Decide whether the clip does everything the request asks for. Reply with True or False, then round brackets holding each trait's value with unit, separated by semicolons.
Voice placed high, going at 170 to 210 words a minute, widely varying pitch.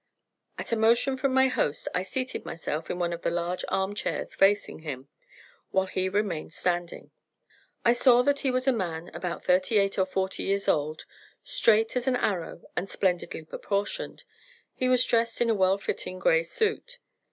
True (200 Hz; 180 wpm; 5.8 semitones)